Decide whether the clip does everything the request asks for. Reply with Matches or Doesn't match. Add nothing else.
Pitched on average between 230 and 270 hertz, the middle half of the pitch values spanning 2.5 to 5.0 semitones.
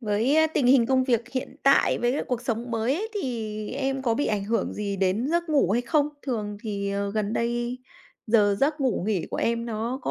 Matches